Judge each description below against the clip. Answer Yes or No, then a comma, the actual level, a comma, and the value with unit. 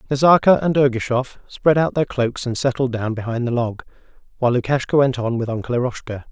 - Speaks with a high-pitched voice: No, low, 125 Hz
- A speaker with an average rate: Yes, average, 190 wpm